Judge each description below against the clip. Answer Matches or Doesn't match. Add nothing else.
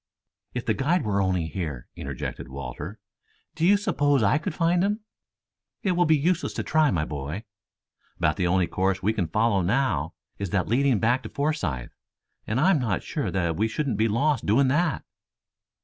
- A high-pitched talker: Doesn't match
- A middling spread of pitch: Doesn't match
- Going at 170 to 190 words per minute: Matches